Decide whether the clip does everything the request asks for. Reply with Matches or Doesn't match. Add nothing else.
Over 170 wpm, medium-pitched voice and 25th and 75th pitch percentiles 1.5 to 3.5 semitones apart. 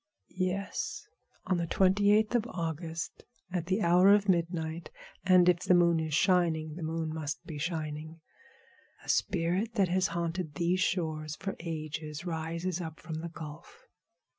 Doesn't match